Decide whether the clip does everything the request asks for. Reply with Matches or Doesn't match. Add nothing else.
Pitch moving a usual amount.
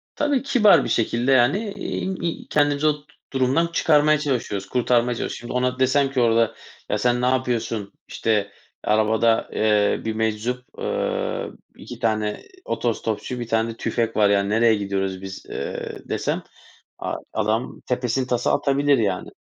Matches